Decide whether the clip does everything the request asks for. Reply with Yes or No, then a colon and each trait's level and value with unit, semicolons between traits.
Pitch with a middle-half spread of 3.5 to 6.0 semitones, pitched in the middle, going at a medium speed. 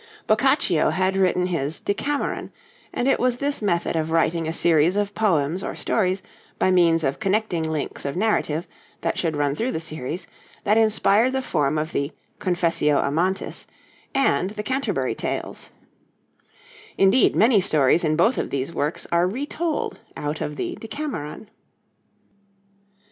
Yes: wide, 5.6 semitones; medium, 180 Hz; average, 150 wpm